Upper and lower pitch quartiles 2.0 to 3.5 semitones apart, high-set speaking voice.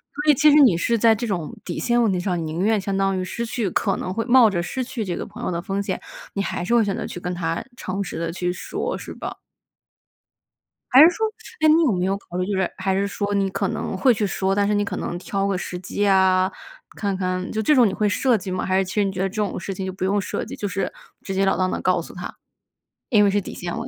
Yes: average, 2.9 semitones; high, 195 Hz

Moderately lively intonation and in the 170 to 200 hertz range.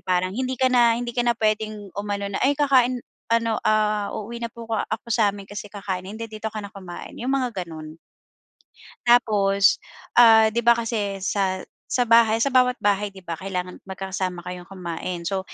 No: average, 3.4 semitones; high, 215 Hz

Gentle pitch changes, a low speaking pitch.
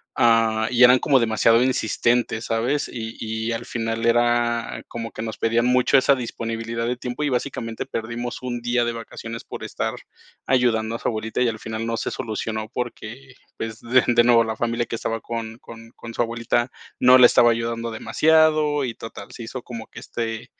Yes: narrow, 1.4 semitones; low, 115 Hz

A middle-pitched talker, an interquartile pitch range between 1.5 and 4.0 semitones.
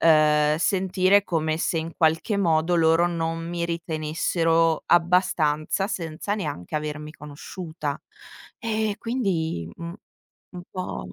Yes: medium, 165 Hz; narrow, 2.6 semitones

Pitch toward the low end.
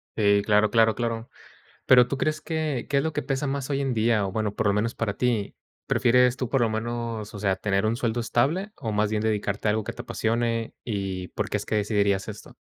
Yes: low, 115 Hz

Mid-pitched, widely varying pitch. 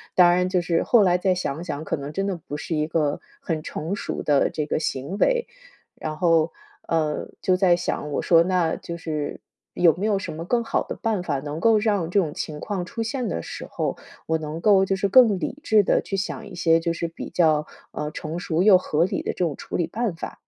No: medium, 175 Hz; average, 3.9 semitones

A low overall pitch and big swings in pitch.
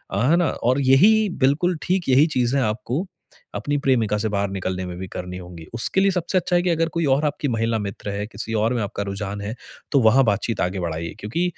Yes: low, 115 Hz; wide, 7.0 semitones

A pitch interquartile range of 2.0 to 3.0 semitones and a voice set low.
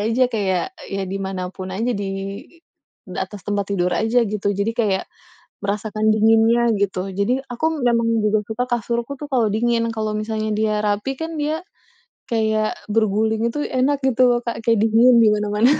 No: narrow, 2.6 semitones; high, 220 Hz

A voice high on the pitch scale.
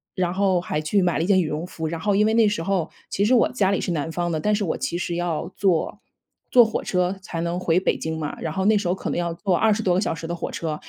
No: medium, 180 Hz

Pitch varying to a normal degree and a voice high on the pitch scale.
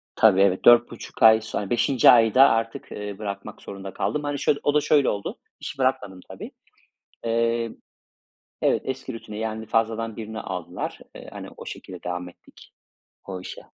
No: average, 3.1 semitones; low, 110 Hz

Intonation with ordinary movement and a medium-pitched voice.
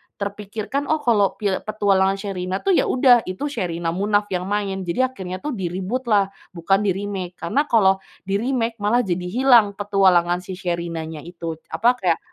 No: average, 3.9 semitones; high, 195 Hz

